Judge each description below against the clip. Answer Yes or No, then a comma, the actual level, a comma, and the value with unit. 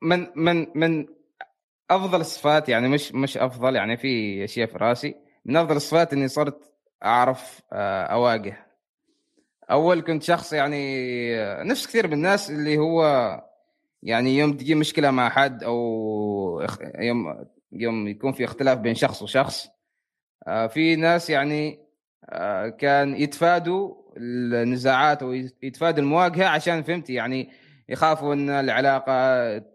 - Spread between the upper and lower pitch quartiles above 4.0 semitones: Yes, average, 4.4 semitones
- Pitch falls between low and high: Yes, medium, 145 Hz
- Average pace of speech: Yes, average, 120 wpm